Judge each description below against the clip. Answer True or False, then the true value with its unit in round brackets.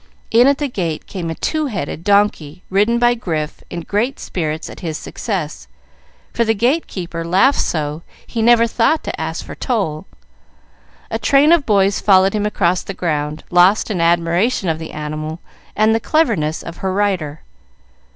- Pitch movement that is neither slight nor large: False (5.9 semitones)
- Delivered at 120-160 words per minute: False (170 wpm)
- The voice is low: False (190 Hz)